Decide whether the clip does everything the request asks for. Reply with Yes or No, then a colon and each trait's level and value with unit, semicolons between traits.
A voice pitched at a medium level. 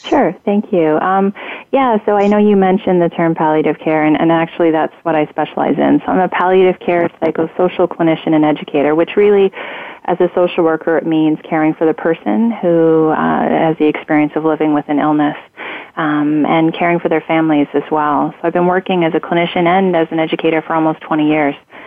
Yes: medium, 165 Hz